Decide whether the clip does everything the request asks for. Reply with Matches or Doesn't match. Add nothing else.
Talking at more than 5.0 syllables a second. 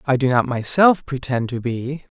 Doesn't match